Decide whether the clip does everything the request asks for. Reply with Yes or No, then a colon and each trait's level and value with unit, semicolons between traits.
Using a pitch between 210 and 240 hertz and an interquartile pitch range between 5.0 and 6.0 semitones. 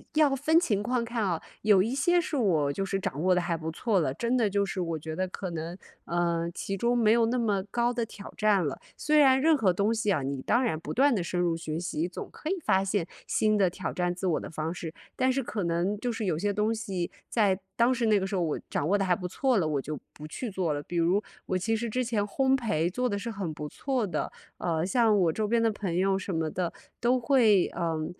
No: high, 195 Hz; average, 5.3 semitones